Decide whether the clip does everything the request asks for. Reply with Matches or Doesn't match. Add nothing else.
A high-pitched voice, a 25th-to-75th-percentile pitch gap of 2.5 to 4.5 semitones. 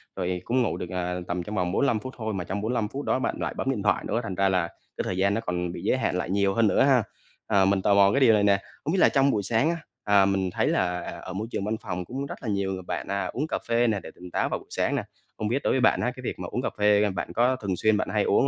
Doesn't match